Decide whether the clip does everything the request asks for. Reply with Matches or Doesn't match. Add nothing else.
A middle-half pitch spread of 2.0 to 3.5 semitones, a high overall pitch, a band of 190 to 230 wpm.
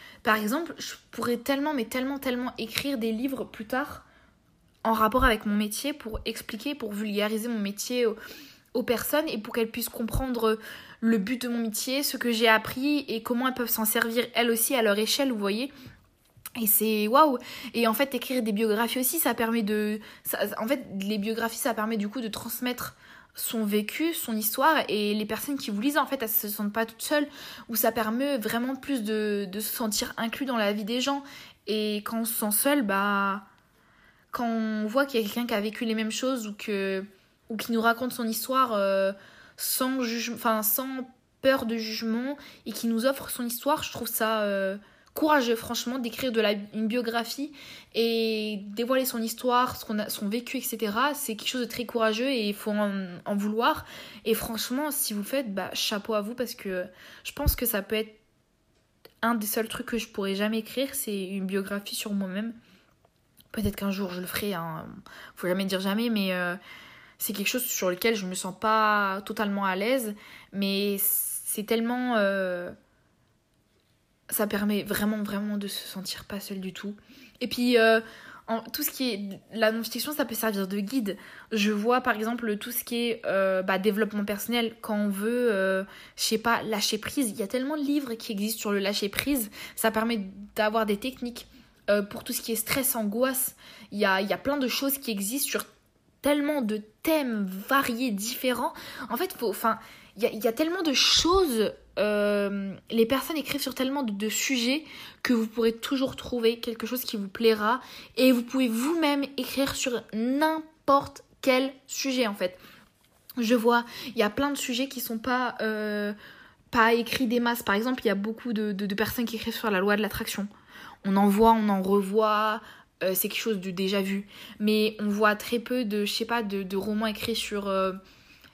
Matches